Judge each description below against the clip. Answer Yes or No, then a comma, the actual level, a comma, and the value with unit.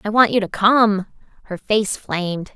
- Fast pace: No, average, 190 wpm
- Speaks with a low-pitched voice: No, high, 205 Hz